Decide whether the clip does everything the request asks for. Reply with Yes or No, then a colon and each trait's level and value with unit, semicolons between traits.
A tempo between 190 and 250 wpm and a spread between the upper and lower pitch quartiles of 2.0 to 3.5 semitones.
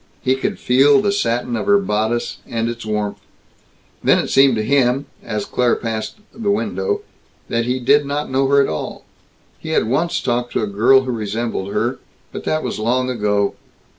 No: average, 195 wpm; average, 4.0 semitones